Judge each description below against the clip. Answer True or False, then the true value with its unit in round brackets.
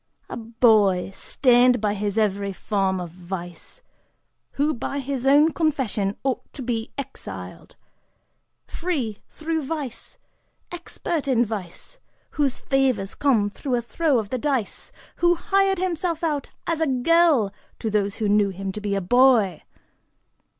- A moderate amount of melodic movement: False (6.4 semitones)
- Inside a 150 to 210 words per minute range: False (140 wpm)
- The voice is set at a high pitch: True (245 Hz)